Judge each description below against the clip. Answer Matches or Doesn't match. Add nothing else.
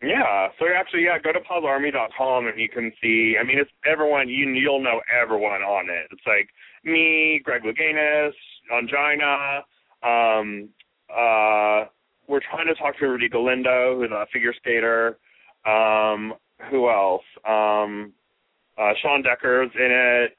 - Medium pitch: Doesn't match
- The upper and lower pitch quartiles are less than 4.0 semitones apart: Doesn't match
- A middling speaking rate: Matches